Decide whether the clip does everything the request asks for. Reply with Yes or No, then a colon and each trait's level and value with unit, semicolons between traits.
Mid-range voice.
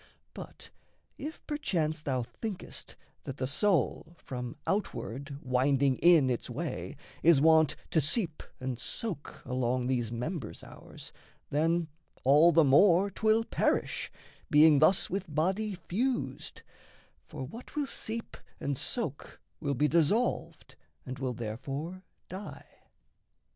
Yes: medium, 155 Hz